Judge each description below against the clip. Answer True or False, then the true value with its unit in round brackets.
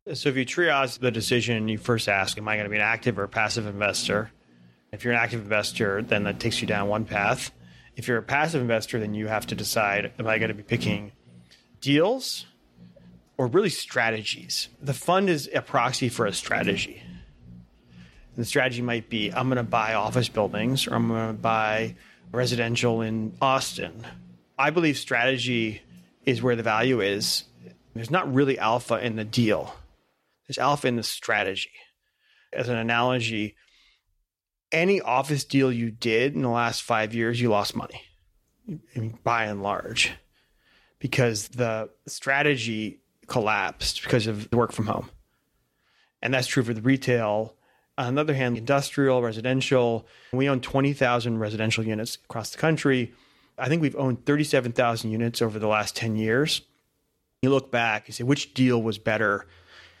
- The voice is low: True (115 Hz)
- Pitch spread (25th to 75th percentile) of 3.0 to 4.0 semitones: True (3.3 semitones)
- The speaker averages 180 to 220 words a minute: False (170 wpm)